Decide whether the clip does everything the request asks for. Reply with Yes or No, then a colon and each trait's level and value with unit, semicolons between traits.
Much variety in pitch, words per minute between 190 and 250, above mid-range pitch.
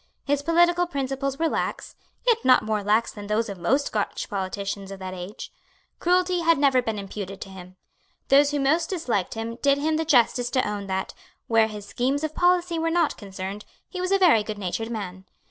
Yes: wide, 7.7 semitones; average, 195 wpm; high, 245 Hz